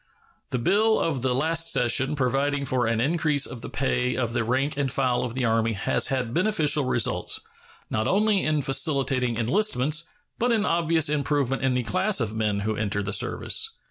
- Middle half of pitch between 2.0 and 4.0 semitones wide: No, average, 4.7 semitones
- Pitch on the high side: No, low, 135 Hz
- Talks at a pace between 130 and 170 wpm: No, average, 185 wpm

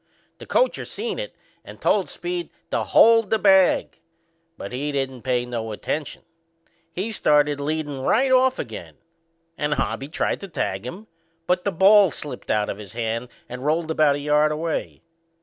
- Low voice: No, medium, 150 Hz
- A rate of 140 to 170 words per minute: Yes, average, 165 wpm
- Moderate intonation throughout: No, wide, 7.4 semitones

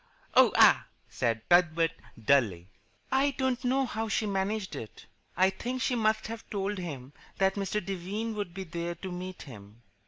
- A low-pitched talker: No, high, 190 Hz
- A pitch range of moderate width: Yes, average, 5.0 semitones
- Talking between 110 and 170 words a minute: Yes, average, 165 wpm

